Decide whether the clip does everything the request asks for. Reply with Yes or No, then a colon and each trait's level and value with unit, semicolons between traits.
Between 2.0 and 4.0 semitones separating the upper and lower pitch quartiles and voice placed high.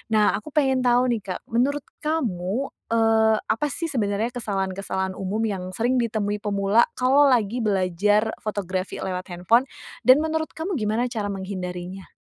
No: average, 4.4 semitones; high, 215 Hz